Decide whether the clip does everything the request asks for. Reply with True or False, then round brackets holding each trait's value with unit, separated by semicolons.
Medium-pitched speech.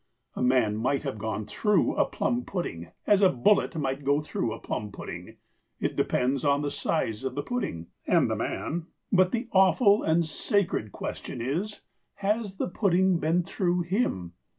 True (160 Hz)